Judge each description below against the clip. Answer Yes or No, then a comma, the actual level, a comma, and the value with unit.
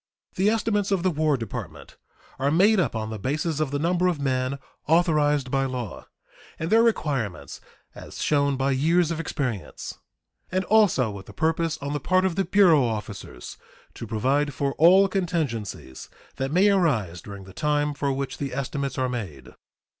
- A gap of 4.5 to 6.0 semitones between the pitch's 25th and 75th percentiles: Yes, average, 5.3 semitones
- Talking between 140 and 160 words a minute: No, average, 175 wpm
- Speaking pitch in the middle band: Yes, medium, 145 Hz